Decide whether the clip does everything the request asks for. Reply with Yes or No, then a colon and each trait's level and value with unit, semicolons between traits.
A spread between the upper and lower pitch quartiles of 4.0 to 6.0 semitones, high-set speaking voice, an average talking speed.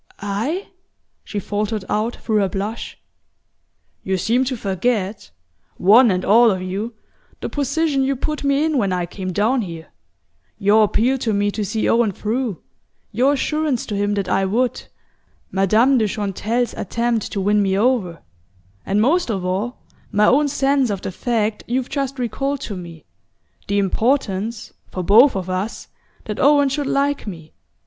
Yes: average, 4.7 semitones; high, 220 Hz; average, 165 wpm